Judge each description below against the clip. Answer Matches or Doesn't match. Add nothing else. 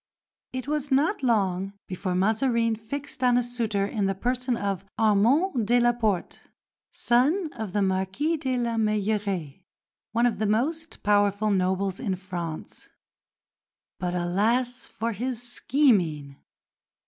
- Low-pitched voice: Doesn't match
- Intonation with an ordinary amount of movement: Matches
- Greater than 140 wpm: Doesn't match